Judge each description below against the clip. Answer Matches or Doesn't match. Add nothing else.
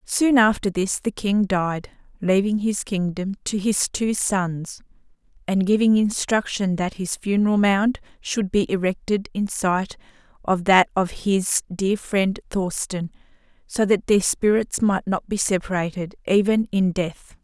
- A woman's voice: Matches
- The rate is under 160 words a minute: Matches